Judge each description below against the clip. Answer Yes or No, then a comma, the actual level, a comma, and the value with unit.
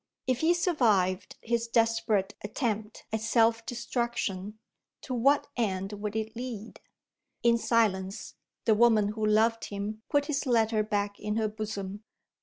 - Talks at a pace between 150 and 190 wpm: No, average, 140 wpm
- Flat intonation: Yes, narrow, 2.2 semitones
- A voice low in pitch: No, high, 220 Hz